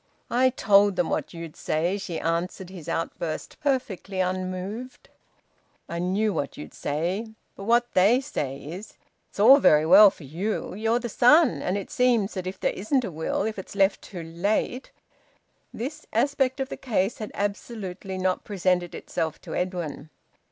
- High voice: Yes, high, 195 Hz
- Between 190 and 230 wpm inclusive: No, average, 170 wpm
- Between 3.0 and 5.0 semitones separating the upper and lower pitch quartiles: Yes, average, 4.5 semitones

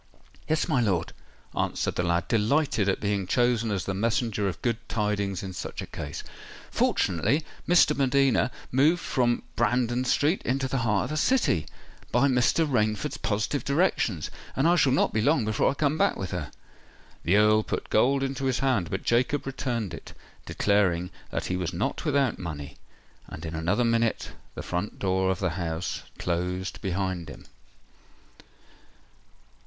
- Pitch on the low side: Yes, low, 110 Hz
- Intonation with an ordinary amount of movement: No, wide, 6.2 semitones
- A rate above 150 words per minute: Yes, average, 165 wpm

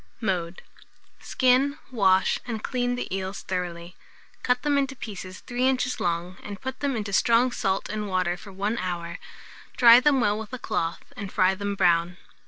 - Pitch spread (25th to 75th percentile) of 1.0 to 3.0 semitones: No, average, 5.1 semitones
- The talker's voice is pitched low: No, high, 205 Hz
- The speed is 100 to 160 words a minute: No, average, 175 wpm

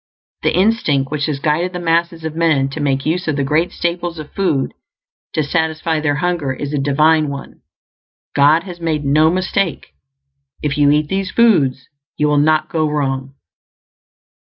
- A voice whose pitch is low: No, medium, 155 Hz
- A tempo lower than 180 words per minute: Yes, average, 170 wpm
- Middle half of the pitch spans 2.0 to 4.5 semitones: Yes, average, 2.9 semitones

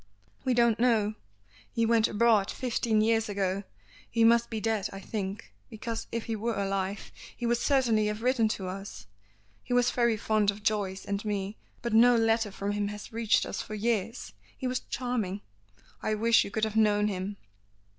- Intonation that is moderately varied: No, narrow, 2.3 semitones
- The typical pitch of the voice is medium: No, high, 220 Hz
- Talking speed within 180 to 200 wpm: Yes, average, 185 wpm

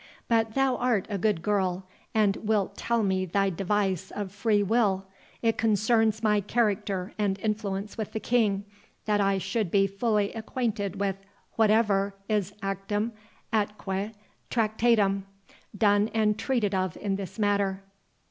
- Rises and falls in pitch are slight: Yes, narrow, 2.0 semitones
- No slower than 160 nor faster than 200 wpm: No, average, 140 wpm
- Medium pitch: No, high, 205 Hz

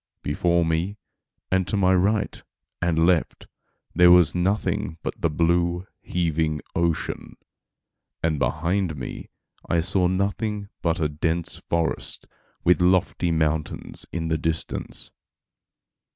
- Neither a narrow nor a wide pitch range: No, narrow, 2.2 semitones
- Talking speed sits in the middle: No, slow, 120 wpm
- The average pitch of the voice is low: Yes, very low, 85 Hz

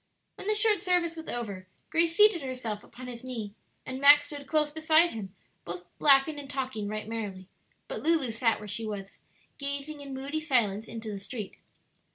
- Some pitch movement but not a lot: No, wide, 6.2 semitones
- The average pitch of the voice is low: No, very high, 260 Hz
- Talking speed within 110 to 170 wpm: No, average, 185 wpm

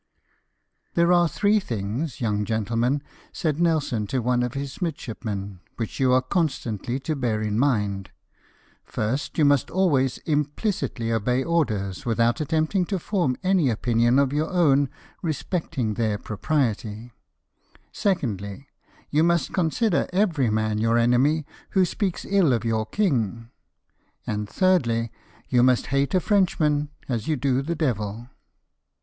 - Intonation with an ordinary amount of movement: No, wide, 6.0 semitones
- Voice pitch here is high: No, low, 130 Hz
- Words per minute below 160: Yes, average, 145 wpm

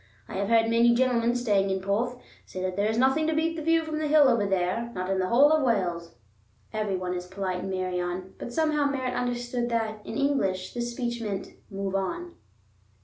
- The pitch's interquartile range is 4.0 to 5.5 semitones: Yes, average, 5.2 semitones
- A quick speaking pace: Yes, fast, 210 wpm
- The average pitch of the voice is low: No, high, 230 Hz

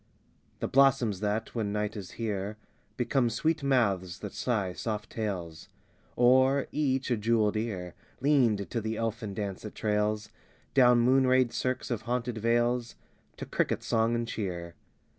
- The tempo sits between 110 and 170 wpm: Yes, average, 150 wpm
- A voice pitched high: No, low, 115 Hz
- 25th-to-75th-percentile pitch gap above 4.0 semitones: No, average, 3.0 semitones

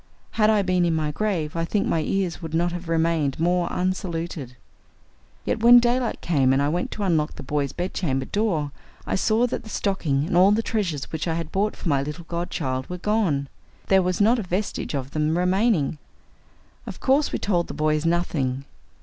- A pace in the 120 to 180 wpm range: No, average, 200 wpm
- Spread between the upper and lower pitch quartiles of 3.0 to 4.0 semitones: No, average, 4.5 semitones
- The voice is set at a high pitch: No, medium, 170 Hz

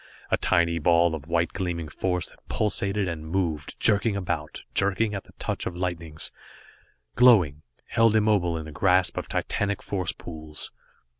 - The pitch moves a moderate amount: Yes, average, 3.6 semitones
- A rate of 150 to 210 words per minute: Yes, average, 155 wpm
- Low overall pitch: Yes, very low, 90 Hz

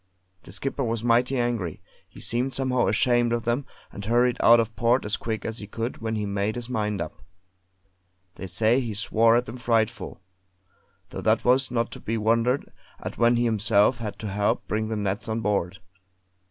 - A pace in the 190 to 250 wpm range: Yes, average, 195 wpm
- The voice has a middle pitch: No, low, 115 Hz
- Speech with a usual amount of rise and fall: No, narrow, 2.2 semitones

